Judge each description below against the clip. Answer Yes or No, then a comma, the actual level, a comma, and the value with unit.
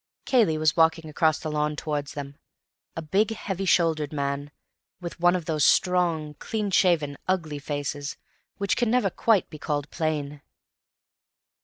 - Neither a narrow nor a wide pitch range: Yes, average, 3.4 semitones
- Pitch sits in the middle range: Yes, medium, 155 Hz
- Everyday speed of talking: Yes, average, 150 wpm